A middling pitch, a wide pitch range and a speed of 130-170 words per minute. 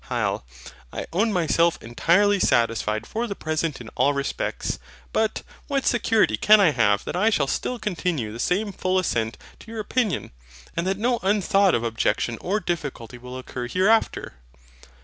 Yes: medium, 175 Hz; wide, 9.0 semitones; average, 165 wpm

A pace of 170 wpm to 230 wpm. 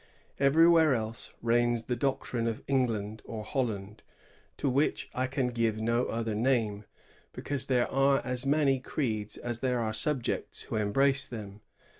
No: average, 150 wpm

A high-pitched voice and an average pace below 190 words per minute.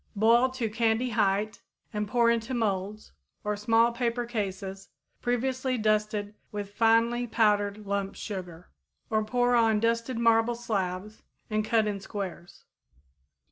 Yes: high, 220 Hz; slow, 135 wpm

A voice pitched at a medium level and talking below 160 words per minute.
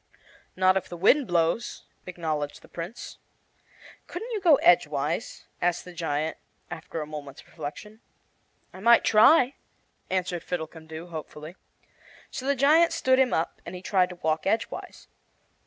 Yes: medium, 175 Hz; average, 140 wpm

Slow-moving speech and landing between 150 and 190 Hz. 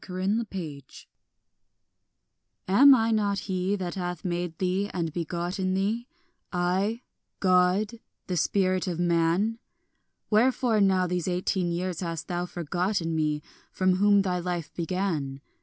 Yes: slow, 130 wpm; medium, 185 Hz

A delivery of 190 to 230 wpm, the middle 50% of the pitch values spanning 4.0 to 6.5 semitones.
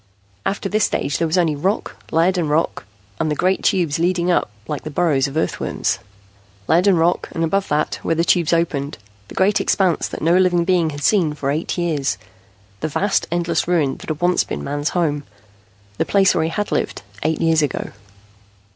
No: average, 200 wpm; average, 2.9 semitones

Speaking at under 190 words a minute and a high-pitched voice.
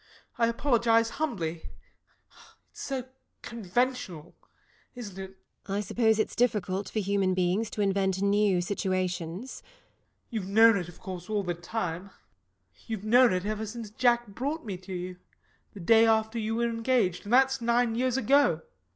Yes: average, 165 wpm; high, 215 Hz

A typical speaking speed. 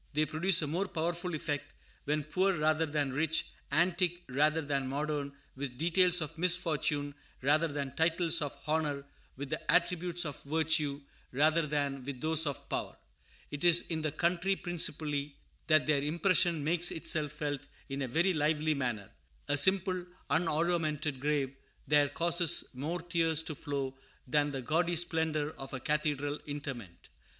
Yes: average, 155 wpm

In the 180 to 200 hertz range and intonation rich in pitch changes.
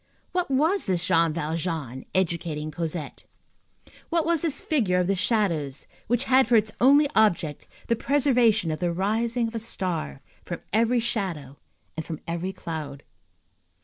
Yes: high, 190 Hz; wide, 6.5 semitones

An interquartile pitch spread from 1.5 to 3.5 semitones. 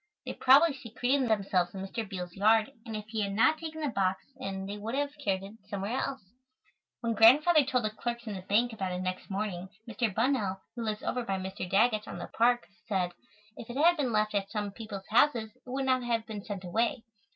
No: average, 4.0 semitones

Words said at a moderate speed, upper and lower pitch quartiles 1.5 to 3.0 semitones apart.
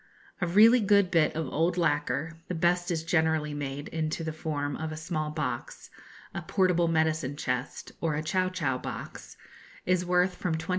Yes: average, 180 wpm; average, 2.7 semitones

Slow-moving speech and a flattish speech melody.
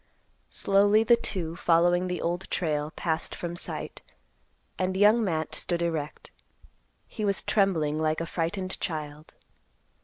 No: slow, 130 wpm; average, 3.5 semitones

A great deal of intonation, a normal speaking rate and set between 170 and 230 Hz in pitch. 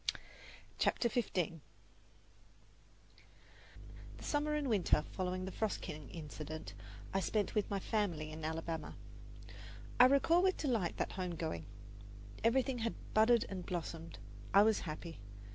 No: wide, 6.1 semitones; slow, 125 wpm; high, 190 Hz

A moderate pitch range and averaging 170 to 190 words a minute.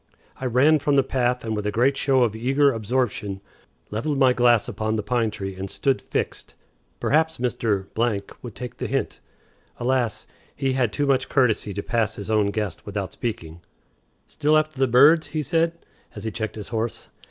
Yes: average, 4.0 semitones; average, 180 wpm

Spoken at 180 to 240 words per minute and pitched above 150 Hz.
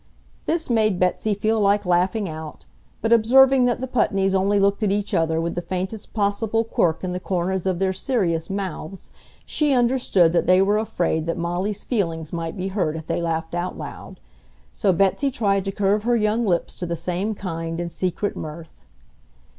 Yes: average, 185 wpm; high, 190 Hz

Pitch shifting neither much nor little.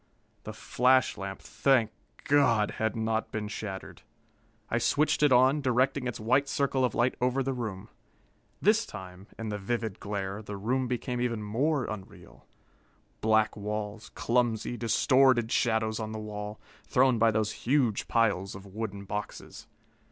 Yes: average, 3.4 semitones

